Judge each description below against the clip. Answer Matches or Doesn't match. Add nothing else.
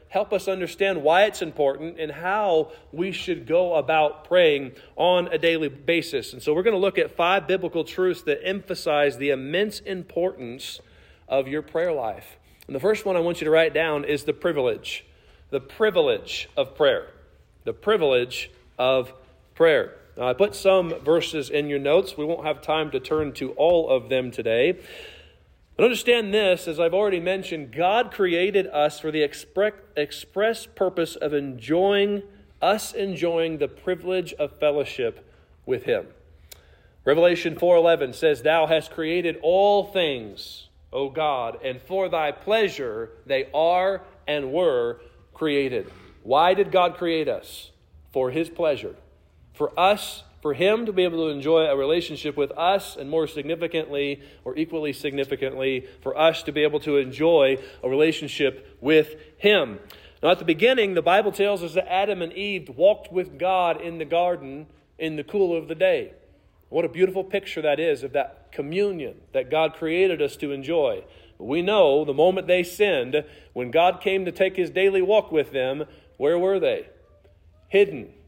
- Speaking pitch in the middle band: Matches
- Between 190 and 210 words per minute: Doesn't match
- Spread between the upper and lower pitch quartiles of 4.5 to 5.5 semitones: Matches